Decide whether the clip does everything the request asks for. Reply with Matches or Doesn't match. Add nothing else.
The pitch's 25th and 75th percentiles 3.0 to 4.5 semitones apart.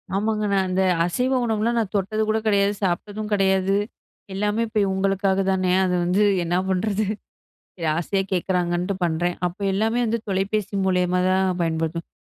Doesn't match